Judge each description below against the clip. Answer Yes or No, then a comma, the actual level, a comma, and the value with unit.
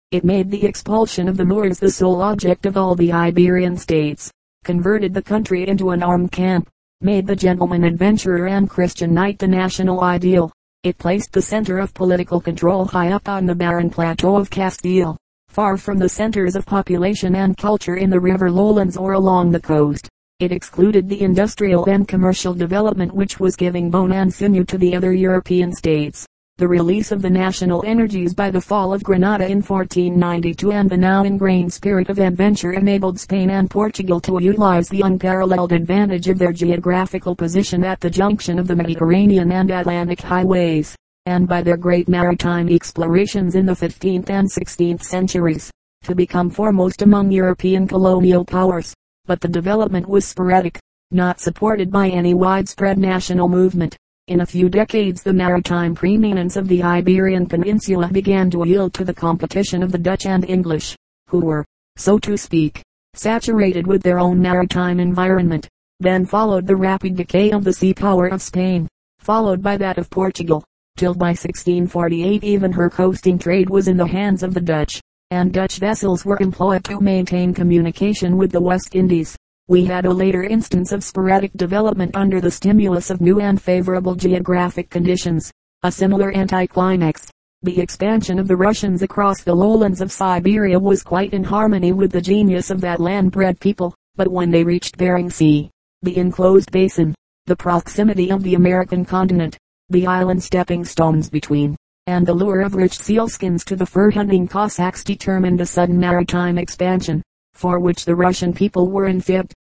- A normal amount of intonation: No, narrow, 1.6 semitones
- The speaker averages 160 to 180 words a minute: Yes, average, 170 wpm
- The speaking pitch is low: No, medium, 185 Hz